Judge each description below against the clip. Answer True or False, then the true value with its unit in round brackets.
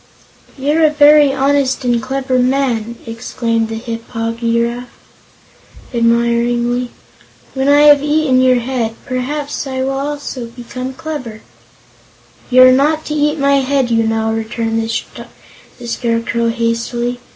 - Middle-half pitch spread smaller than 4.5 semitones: True (3.1 semitones)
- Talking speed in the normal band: False (130 wpm)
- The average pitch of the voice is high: True (250 Hz)